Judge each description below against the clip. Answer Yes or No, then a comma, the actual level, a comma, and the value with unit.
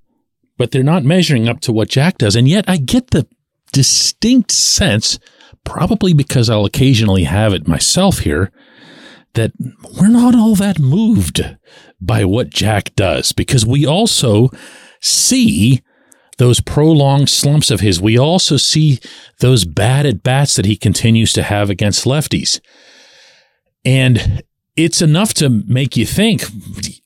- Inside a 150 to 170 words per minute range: No, average, 140 wpm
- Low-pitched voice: Yes, low, 130 Hz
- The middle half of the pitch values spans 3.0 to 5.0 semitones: No, wide, 5.6 semitones